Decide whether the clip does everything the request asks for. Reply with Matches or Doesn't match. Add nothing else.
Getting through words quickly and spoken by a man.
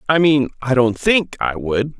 Matches